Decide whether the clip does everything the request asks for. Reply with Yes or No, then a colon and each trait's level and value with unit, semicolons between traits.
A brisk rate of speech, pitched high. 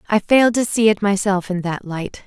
Yes: fast, 240 wpm; high, 200 Hz